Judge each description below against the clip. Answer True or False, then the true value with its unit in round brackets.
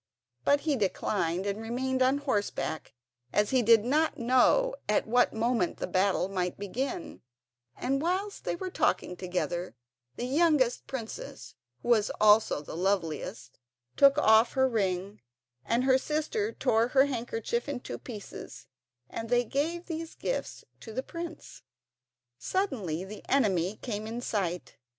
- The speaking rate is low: False (145 wpm)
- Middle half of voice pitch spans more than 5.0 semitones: True (5.5 semitones)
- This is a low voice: False (235 Hz)